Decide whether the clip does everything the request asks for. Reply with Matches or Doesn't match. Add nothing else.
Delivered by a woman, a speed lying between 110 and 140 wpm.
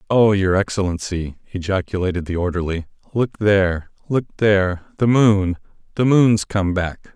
Doesn't match